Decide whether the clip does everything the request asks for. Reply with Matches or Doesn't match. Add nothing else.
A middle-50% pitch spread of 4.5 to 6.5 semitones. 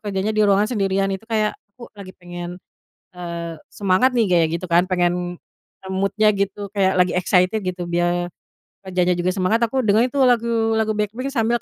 Doesn't match